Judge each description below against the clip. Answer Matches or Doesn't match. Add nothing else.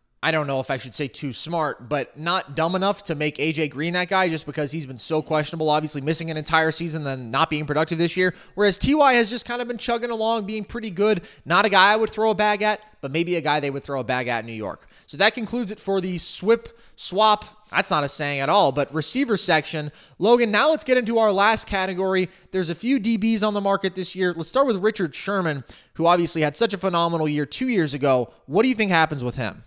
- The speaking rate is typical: Doesn't match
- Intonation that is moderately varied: Doesn't match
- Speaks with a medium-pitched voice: Matches